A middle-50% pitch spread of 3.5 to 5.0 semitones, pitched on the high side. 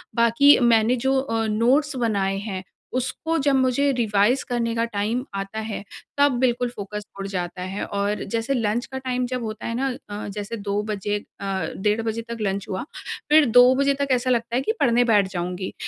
Yes: average, 3.8 semitones; high, 230 Hz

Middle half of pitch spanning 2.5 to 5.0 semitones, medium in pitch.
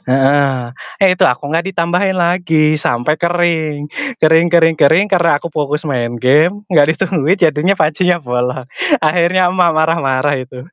Yes: average, 3.7 semitones; medium, 160 Hz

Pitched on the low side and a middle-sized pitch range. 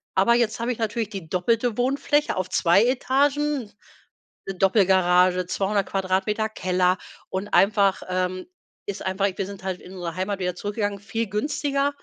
No: high, 200 Hz; average, 3.6 semitones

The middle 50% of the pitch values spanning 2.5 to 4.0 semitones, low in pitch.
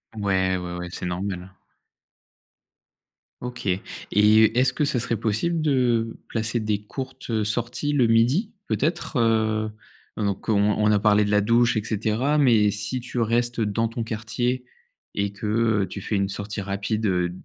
Yes: average, 2.8 semitones; low, 110 Hz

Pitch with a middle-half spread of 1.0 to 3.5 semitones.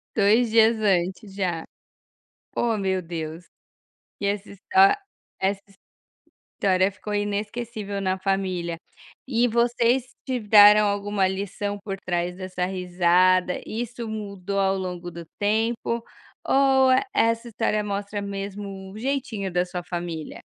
Yes: average, 3.1 semitones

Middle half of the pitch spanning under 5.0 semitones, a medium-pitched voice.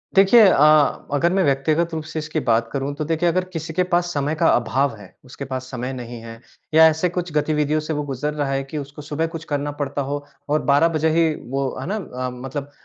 Yes: average, 2.8 semitones; medium, 145 Hz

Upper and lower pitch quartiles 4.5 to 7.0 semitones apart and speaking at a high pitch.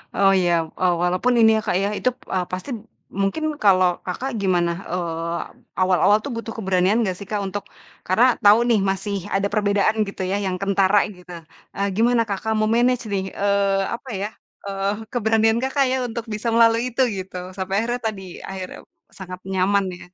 No: average, 3.0 semitones; high, 200 Hz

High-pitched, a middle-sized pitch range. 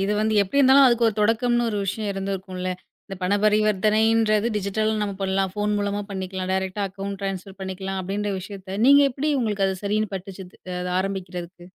No: high, 200 Hz; narrow, 2.0 semitones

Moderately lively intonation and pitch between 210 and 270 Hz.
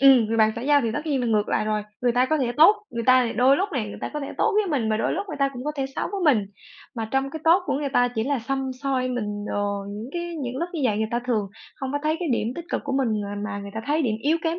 Yes: average, 5.0 semitones; very high, 255 Hz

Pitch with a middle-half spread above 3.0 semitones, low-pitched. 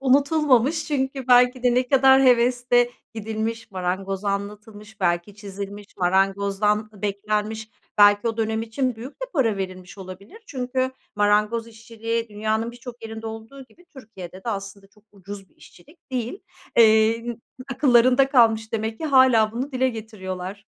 No: average, 3.5 semitones; high, 225 Hz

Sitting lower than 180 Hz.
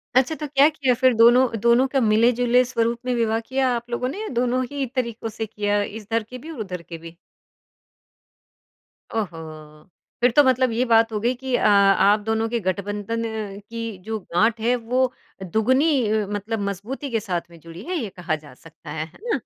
No: high, 230 Hz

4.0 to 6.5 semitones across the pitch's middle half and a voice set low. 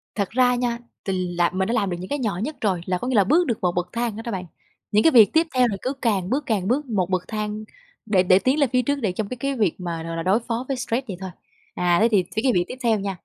No: average, 5.1 semitones; high, 215 Hz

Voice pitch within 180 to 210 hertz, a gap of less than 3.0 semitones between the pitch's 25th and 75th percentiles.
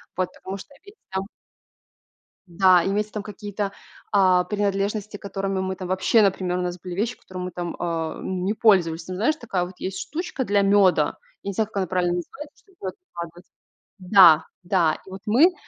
Yes: high, 190 Hz; narrow, 2.4 semitones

